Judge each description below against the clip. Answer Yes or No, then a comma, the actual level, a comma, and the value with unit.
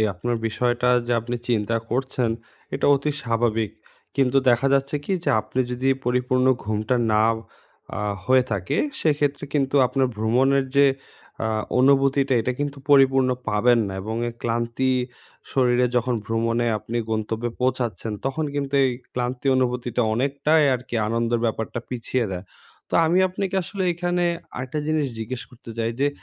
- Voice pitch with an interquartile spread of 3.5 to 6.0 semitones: No, average, 2.9 semitones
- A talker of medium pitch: No, low, 125 Hz